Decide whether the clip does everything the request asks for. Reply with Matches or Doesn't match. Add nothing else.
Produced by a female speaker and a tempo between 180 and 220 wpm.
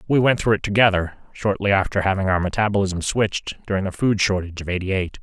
Doesn't match